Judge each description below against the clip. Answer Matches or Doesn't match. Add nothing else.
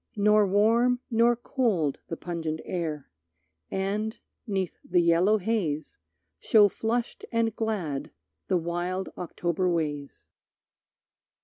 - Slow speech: Matches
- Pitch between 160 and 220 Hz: Matches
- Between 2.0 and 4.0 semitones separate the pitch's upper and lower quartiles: Doesn't match